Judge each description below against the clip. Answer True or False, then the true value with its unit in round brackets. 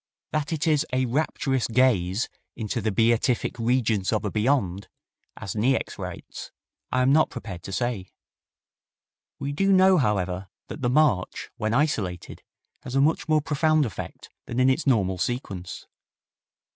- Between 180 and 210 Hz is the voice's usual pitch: False (125 Hz)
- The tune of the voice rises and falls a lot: True (5.7 semitones)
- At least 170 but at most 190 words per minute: False (150 wpm)